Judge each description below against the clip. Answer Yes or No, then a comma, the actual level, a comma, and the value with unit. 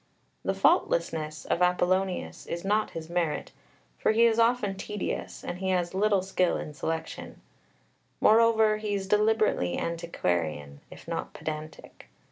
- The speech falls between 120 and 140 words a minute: Yes, slow, 135 wpm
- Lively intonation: No, average, 4.7 semitones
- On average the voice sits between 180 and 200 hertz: Yes, medium, 185 Hz